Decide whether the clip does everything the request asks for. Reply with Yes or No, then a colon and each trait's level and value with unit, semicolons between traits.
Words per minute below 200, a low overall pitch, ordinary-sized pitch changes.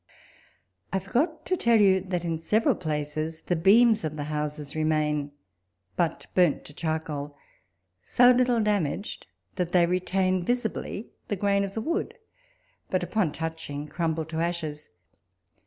No: average, 140 wpm; medium, 175 Hz; average, 4.6 semitones